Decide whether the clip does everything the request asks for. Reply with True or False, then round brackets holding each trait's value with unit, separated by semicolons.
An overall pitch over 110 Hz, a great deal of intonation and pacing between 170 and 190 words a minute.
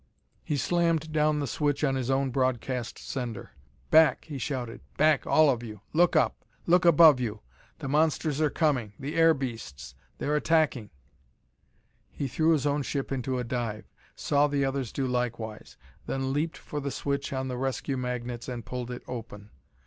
False (135 Hz; 3.4 semitones; 175 wpm)